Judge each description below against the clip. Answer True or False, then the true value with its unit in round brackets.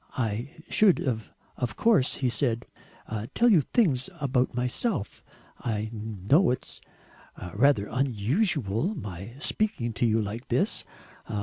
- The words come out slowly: True (120 wpm)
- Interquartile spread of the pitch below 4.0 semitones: False (5.1 semitones)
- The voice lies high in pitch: False (125 Hz)